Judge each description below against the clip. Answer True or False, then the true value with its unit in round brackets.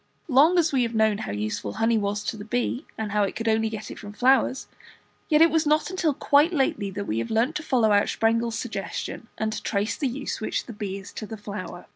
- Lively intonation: False (4.4 semitones)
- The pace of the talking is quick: True (245 wpm)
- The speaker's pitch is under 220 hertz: False (225 Hz)